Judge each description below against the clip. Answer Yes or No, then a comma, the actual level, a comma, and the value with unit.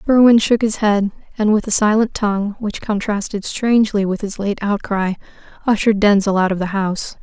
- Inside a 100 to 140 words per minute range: No, average, 185 wpm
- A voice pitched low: No, high, 205 Hz